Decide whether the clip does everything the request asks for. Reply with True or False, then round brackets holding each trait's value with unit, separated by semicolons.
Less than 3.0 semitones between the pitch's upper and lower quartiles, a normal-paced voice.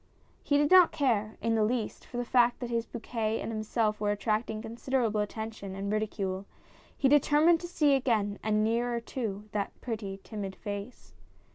True (2.6 semitones; 170 wpm)